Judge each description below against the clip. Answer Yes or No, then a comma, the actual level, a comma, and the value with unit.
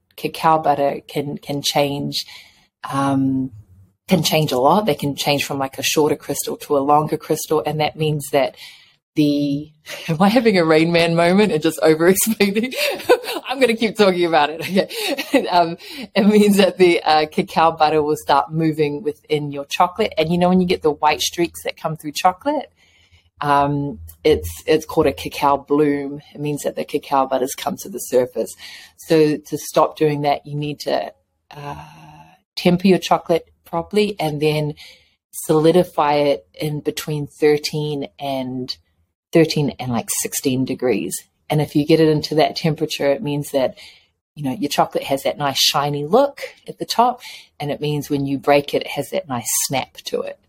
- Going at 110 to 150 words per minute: No, average, 180 wpm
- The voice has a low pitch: No, medium, 150 Hz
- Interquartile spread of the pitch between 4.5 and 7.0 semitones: No, average, 3.1 semitones